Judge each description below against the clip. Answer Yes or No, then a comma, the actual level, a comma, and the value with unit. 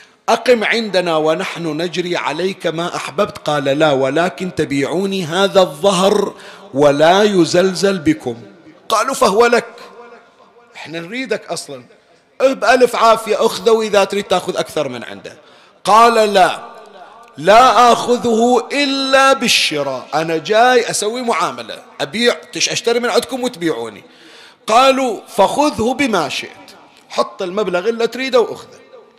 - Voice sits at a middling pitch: No, high, 200 Hz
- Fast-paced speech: No, average, 115 wpm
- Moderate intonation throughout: No, wide, 6.1 semitones